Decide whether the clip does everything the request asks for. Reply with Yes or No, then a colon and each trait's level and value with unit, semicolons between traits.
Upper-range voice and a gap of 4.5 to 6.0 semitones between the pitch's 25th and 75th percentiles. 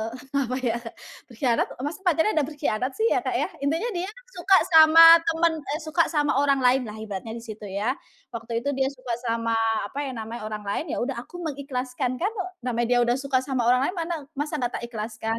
Yes: very high, 260 Hz; average, 4.8 semitones